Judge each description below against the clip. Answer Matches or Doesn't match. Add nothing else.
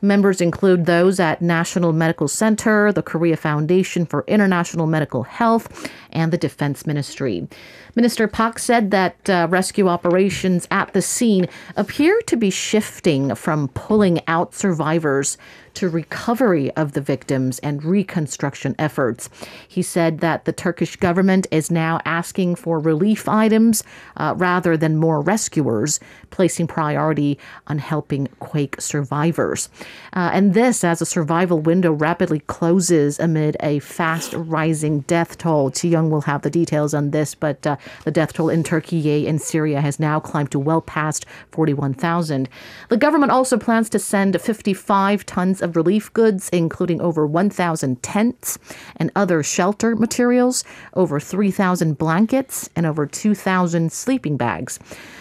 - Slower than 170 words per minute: Matches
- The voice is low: Doesn't match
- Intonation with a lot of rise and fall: Doesn't match